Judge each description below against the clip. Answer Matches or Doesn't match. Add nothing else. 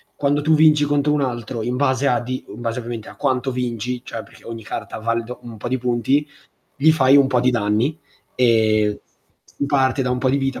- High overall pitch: Doesn't match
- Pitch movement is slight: Doesn't match